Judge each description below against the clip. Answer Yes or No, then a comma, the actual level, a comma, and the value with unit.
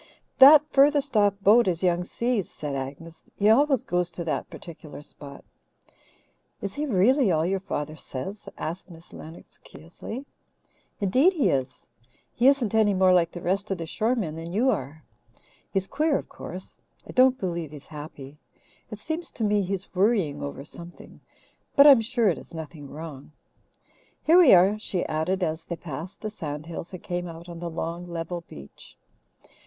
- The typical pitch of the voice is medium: Yes, medium, 180 Hz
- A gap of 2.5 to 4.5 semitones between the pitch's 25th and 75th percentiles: No, wide, 5.4 semitones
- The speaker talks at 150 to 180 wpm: Yes, average, 175 wpm